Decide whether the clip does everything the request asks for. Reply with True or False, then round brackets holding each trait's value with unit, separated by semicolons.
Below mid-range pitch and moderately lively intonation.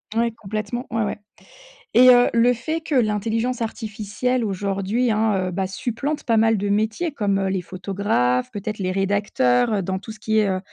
False (215 Hz; 3.0 semitones)